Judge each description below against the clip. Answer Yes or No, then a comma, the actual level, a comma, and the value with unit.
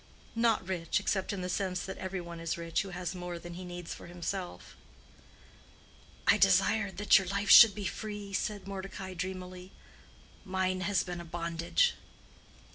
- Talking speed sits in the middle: Yes, average, 160 wpm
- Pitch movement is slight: Yes, narrow, 2.0 semitones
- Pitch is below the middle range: No, medium, 185 Hz